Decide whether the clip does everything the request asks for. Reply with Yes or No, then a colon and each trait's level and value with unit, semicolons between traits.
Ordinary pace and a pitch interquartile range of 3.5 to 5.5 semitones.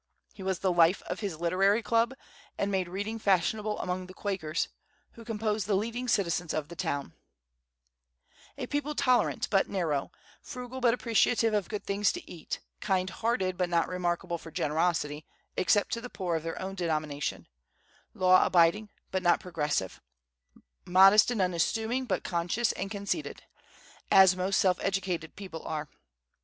Yes: average, 155 wpm; average, 3.8 semitones